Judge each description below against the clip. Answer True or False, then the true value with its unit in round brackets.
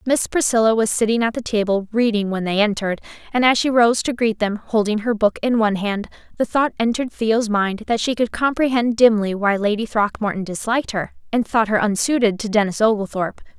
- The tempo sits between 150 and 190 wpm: False (205 wpm)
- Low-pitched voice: False (220 Hz)